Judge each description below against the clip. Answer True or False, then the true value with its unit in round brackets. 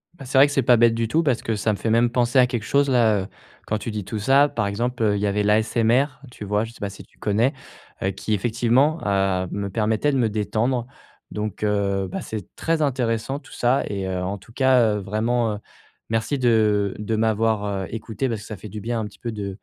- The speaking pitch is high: False (110 Hz)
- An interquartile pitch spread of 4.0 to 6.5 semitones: False (2.9 semitones)